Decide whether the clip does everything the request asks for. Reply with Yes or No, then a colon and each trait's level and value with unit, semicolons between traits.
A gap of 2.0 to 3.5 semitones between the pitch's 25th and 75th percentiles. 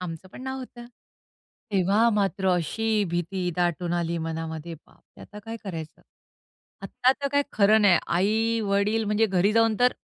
No: average, 4.3 semitones